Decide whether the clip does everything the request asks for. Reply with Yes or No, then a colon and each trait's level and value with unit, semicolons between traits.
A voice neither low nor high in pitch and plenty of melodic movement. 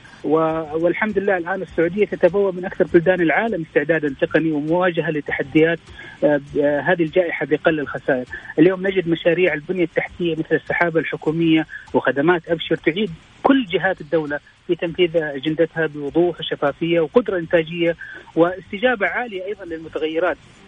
No: medium, 170 Hz; narrow, 2.5 semitones